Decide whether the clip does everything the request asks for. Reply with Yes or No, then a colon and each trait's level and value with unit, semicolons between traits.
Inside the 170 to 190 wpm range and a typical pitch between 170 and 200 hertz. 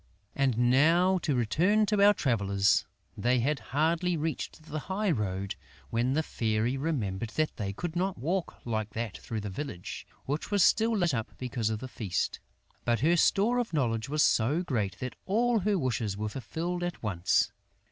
No: average, 180 wpm; low, 135 Hz